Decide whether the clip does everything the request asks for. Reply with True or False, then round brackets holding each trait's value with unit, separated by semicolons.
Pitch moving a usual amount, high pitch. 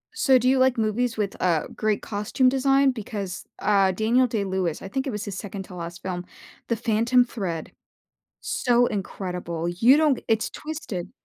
True (5.0 semitones; 215 Hz)